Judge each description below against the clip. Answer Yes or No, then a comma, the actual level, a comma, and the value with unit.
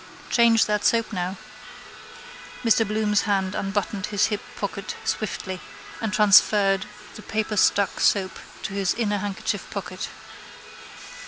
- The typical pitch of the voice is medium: No, high, 205 Hz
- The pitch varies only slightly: Yes, narrow, 1.7 semitones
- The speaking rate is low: Yes, slow, 115 wpm